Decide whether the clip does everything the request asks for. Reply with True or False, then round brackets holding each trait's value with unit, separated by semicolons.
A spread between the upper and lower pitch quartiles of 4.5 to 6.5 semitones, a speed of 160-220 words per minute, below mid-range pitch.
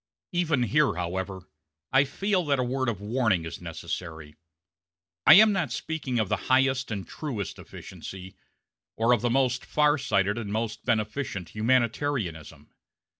False (5.6 semitones; 145 wpm; 120 Hz)